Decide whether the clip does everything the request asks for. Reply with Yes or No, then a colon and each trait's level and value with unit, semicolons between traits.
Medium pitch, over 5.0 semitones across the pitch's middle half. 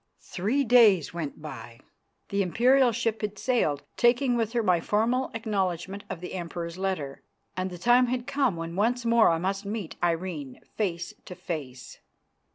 No: high, 195 Hz; wide, 5.6 semitones